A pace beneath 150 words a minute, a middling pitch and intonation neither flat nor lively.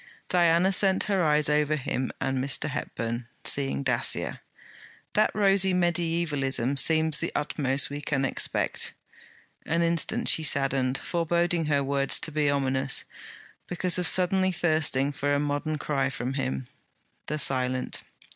Yes: slow, 135 wpm; medium, 150 Hz; average, 3.9 semitones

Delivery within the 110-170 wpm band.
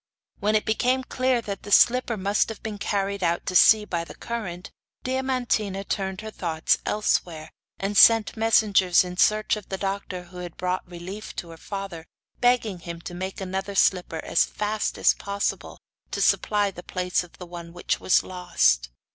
No: average, 180 wpm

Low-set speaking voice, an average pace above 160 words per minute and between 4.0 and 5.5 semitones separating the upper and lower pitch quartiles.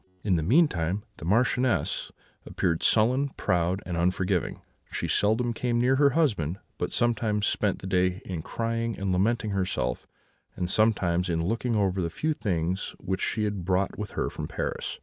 Yes: low, 100 Hz; average, 170 wpm; average, 4.3 semitones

